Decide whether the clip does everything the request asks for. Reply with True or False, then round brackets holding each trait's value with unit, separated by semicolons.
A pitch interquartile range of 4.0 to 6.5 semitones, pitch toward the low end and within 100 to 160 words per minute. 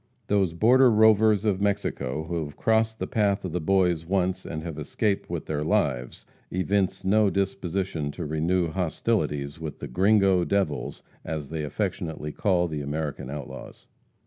True (4.5 semitones; 90 Hz; 155 wpm)